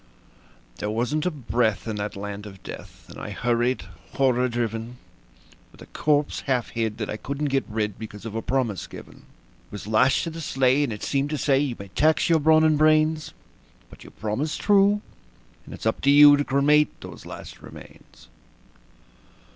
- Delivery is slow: No, average, 185 wpm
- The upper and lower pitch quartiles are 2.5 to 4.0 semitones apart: No, average, 5.1 semitones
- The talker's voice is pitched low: Yes, low, 130 Hz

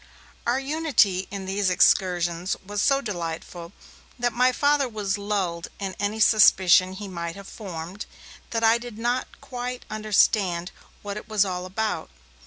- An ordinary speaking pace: Yes, average, 150 wpm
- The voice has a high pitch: Yes, high, 205 Hz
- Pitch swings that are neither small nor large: Yes, average, 3.9 semitones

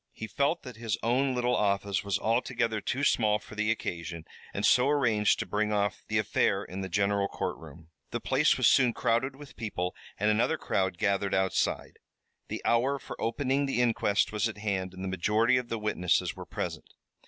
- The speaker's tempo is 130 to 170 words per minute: No, average, 190 wpm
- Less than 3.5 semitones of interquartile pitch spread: No, average, 3.8 semitones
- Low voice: Yes, low, 110 Hz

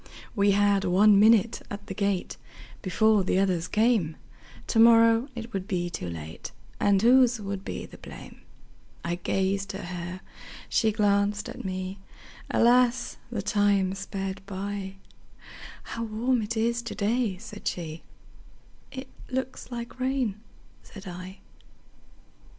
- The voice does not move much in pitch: No, average, 3.2 semitones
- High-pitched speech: Yes, high, 205 Hz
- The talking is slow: Yes, slow, 115 wpm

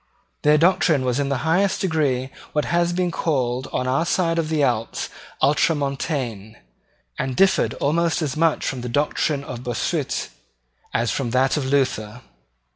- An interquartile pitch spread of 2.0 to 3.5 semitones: No, average, 4.3 semitones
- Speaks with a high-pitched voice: No, medium, 140 Hz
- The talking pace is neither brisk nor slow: Yes, average, 155 wpm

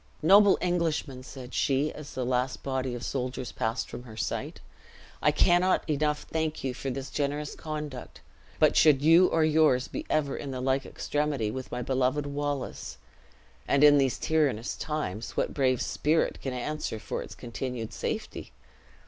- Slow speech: No, average, 165 wpm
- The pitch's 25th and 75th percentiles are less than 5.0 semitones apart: Yes, average, 3.1 semitones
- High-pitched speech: No, medium, 140 Hz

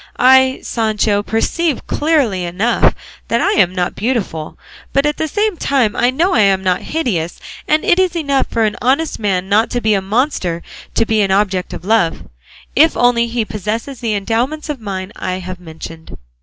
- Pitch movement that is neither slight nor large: No, wide, 5.9 semitones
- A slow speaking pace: No, average, 185 wpm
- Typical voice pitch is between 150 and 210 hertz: No, high, 225 Hz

